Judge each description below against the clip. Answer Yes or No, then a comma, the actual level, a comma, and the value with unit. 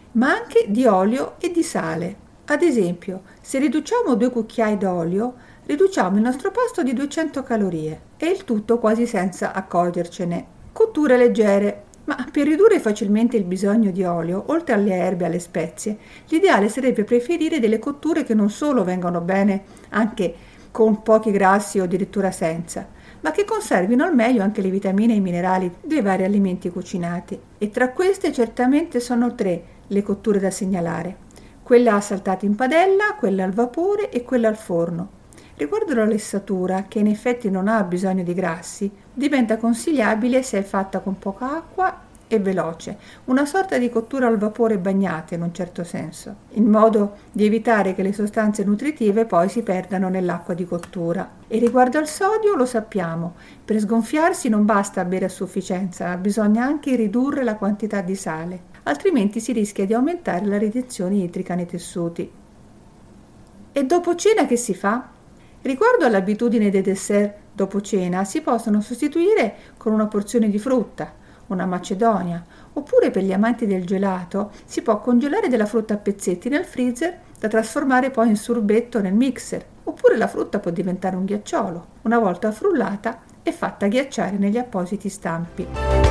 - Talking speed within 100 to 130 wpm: No, average, 160 wpm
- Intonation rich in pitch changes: No, average, 4.7 semitones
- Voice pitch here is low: No, high, 215 Hz